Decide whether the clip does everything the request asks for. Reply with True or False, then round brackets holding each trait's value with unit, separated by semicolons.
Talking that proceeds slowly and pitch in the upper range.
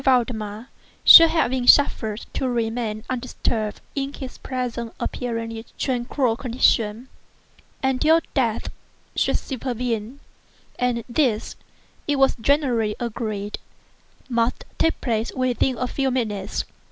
True (105 wpm; 240 Hz)